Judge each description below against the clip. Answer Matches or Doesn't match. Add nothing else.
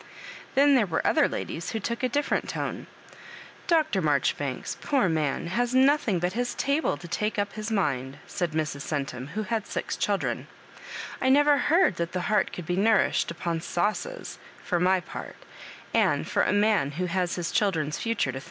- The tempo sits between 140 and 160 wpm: Doesn't match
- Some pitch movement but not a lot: Doesn't match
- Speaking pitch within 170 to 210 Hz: Matches